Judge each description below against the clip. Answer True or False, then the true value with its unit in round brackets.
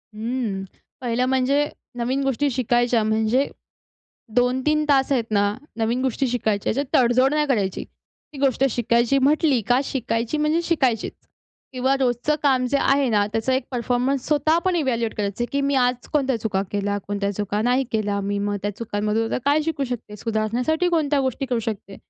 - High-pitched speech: True (245 Hz)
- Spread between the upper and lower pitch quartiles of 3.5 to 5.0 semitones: True (3.8 semitones)